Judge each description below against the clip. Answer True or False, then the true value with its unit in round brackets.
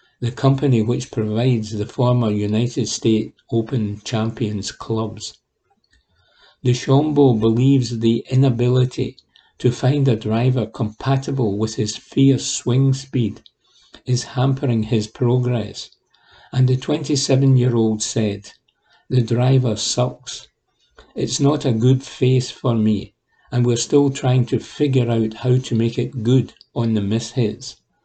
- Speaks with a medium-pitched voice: False (120 Hz)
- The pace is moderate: False (125 wpm)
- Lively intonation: False (2.7 semitones)